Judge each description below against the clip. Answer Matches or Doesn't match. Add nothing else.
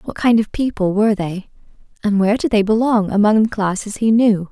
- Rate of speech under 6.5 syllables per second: Matches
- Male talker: Doesn't match